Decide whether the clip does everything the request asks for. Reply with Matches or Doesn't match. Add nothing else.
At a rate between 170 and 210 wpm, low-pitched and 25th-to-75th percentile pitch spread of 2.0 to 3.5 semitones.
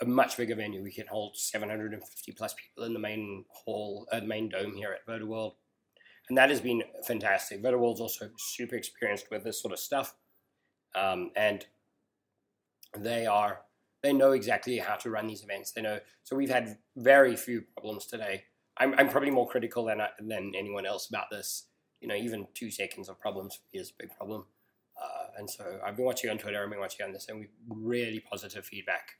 Matches